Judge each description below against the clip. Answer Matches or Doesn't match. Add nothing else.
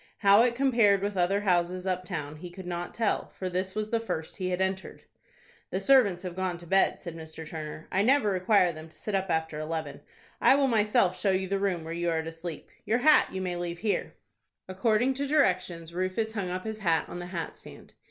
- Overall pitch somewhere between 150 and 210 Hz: Matches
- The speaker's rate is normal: Doesn't match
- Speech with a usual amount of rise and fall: Matches